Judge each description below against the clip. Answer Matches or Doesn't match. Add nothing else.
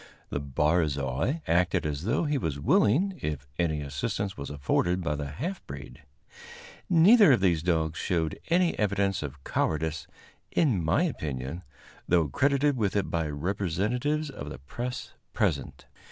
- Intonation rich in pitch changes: Matches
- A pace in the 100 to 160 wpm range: Matches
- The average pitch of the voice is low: Matches